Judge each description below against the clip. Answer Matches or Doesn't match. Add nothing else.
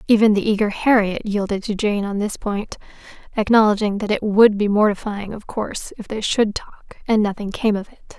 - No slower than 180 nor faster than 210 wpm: Matches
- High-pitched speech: Matches